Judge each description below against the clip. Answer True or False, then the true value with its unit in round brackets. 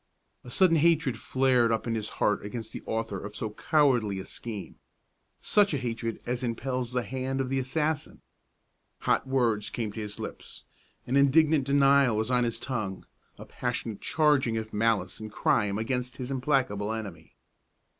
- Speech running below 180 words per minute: True (165 wpm)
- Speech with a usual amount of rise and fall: True (3.4 semitones)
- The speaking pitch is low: True (125 Hz)